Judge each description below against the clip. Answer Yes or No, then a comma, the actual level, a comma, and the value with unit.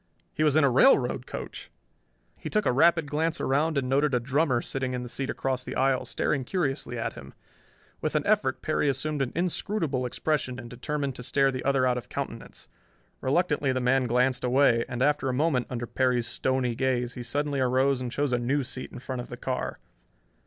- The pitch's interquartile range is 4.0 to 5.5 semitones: No, narrow, 2.6 semitones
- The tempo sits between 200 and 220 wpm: Yes, fast, 205 wpm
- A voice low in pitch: Yes, low, 130 Hz